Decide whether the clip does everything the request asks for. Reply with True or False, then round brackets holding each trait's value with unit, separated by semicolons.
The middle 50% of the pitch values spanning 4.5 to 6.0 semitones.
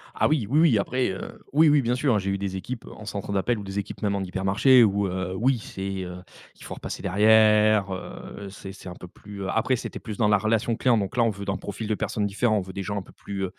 False (2.8 semitones)